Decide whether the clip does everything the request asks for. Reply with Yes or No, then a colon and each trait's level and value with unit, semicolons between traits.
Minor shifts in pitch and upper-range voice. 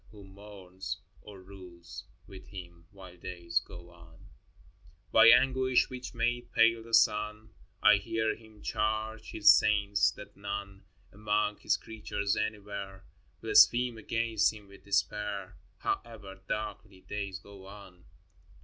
No: narrow, 2.2 semitones; low, 100 Hz